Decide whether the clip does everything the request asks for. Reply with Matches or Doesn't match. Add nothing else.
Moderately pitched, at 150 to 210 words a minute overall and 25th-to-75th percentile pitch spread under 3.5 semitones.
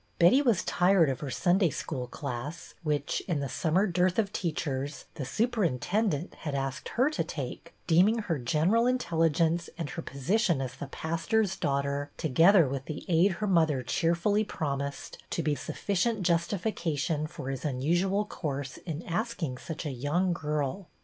Doesn't match